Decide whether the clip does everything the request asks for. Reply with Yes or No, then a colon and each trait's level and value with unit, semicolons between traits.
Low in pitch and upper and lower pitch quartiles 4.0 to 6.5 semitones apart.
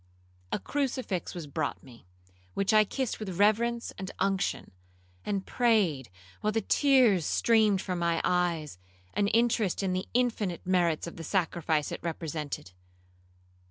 No: high, 190 Hz; average, 4.6 semitones